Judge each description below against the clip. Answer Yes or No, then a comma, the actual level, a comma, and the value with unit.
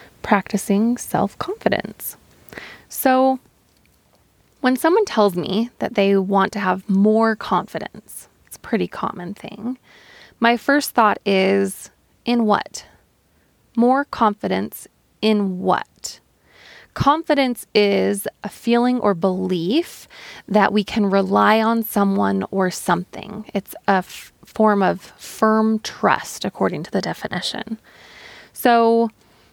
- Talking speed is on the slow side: Yes, slow, 115 wpm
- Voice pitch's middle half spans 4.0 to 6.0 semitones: No, average, 3.2 semitones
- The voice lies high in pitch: Yes, high, 210 Hz